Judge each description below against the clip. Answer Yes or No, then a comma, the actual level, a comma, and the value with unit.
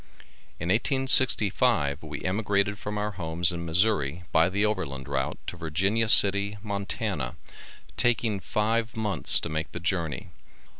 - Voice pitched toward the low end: Yes, very low, 95 Hz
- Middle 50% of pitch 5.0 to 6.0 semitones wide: No, average, 4.5 semitones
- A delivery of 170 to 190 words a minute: No, slow, 135 wpm